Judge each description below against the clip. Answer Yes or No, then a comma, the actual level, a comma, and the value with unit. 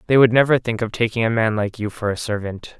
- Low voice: Yes, low, 115 Hz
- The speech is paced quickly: Yes, fast, 280 wpm